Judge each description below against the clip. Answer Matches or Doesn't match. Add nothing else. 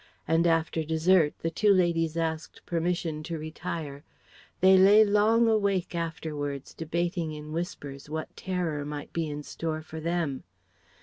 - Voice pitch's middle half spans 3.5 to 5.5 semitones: Doesn't match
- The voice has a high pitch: Doesn't match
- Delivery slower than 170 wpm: Matches